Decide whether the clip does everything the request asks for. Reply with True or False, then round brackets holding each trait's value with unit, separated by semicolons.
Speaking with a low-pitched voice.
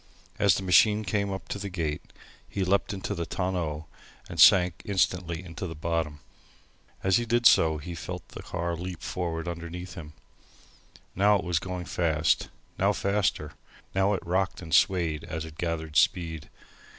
True (90 Hz)